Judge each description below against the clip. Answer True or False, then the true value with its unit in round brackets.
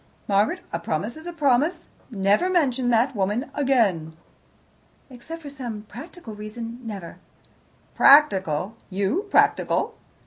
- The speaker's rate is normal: False (115 wpm)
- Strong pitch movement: True (6.2 semitones)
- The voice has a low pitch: False (235 Hz)